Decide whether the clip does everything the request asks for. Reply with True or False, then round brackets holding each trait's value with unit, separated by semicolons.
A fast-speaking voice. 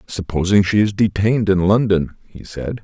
False (170 wpm)